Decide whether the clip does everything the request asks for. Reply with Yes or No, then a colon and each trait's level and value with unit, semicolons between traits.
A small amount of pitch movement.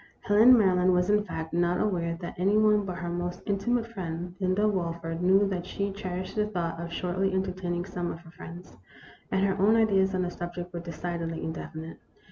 Yes: narrow, 2.3 semitones